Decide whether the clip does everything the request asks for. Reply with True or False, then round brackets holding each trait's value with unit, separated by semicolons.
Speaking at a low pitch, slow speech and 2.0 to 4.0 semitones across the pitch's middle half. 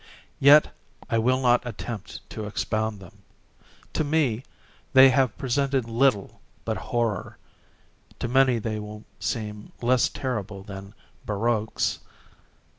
True (115 Hz; 115 wpm; 3.6 semitones)